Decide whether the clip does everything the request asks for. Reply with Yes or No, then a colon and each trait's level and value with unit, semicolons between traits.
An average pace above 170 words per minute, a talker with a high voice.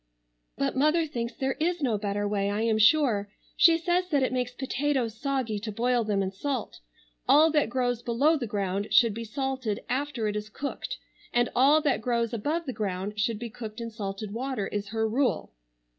Yes: average, 195 wpm; high, 235 Hz